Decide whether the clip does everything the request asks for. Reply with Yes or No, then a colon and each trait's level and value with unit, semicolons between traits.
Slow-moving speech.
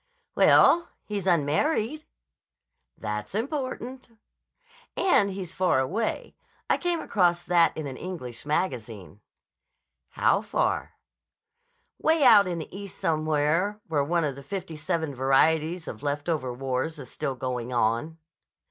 Yes: slow, 130 wpm